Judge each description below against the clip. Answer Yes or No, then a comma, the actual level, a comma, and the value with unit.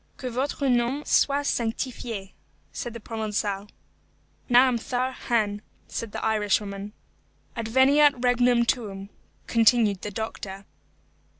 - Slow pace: Yes, slow, 100 wpm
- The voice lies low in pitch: No, high, 230 Hz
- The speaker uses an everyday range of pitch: Yes, average, 3.2 semitones